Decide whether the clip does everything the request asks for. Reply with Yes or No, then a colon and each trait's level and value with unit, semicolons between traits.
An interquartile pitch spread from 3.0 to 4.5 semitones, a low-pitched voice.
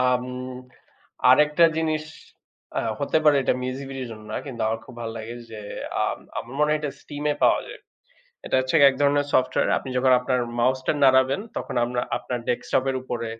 No: narrow, 2.6 semitones; low, 130 Hz